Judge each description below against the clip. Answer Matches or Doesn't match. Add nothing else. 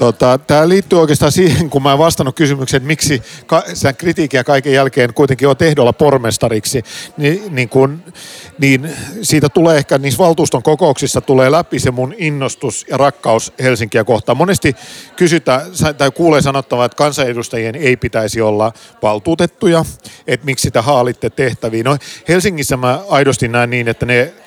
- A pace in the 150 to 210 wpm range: Matches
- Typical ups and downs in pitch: Matches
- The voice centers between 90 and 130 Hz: Doesn't match